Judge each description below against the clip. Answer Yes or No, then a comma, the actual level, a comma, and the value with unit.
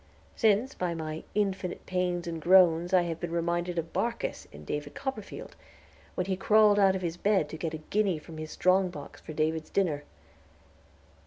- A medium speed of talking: Yes, average, 180 wpm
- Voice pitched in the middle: Yes, medium, 175 Hz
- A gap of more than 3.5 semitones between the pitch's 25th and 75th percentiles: No, average, 3.1 semitones